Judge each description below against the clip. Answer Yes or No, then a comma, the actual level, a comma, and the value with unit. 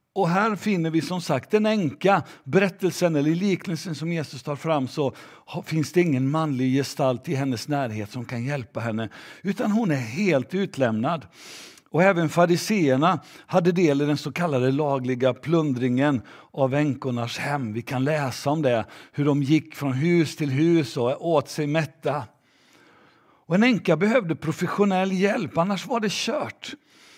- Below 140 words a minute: No, average, 160 wpm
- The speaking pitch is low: No, medium, 155 Hz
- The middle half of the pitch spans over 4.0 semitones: Yes, average, 5.1 semitones